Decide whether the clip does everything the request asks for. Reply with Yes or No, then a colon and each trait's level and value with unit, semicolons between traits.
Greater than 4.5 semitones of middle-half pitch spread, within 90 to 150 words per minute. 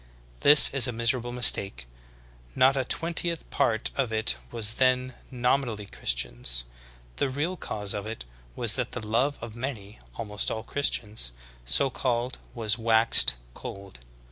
No: average, 3.7 semitones; average, 145 wpm